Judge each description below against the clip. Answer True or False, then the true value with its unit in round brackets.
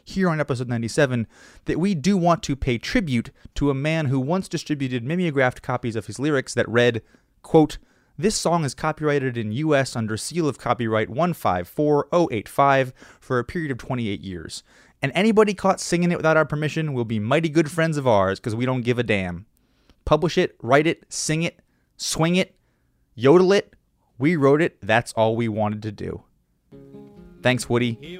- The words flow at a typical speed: True (180 wpm)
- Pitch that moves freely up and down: True (5.8 semitones)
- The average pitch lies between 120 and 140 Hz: True (135 Hz)